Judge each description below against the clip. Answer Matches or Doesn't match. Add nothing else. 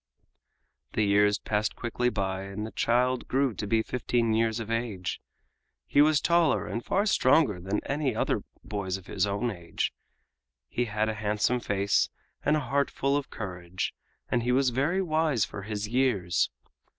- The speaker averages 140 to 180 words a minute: Matches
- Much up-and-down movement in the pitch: Doesn't match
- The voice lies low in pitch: Matches